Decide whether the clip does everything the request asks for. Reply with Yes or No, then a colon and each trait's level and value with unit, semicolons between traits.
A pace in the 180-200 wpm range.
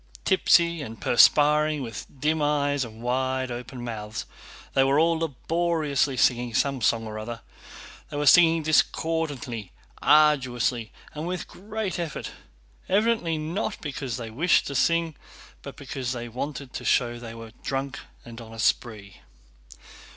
No: average, 145 wpm